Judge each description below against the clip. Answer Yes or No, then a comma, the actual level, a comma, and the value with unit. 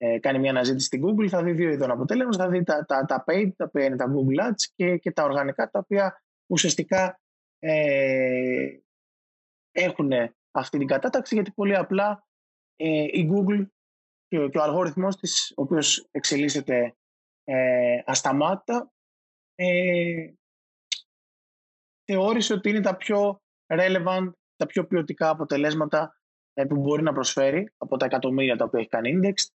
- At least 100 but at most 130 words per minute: No, average, 150 wpm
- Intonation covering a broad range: Yes, wide, 5.9 semitones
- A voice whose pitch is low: No, medium, 170 Hz